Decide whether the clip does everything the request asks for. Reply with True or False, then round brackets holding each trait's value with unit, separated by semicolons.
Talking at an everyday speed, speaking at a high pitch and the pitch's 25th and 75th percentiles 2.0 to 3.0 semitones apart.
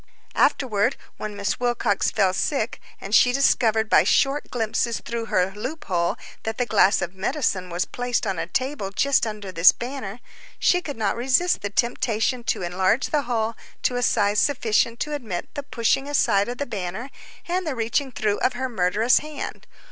False (180 wpm; 230 Hz; 4.5 semitones)